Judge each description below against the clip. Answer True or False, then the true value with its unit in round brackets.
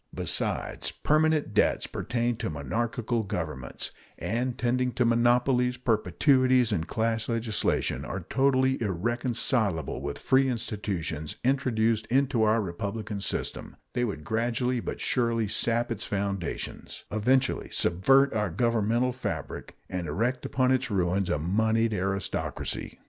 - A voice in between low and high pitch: False (115 Hz)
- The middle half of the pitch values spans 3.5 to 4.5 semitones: True (3.9 semitones)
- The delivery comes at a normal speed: False (120 wpm)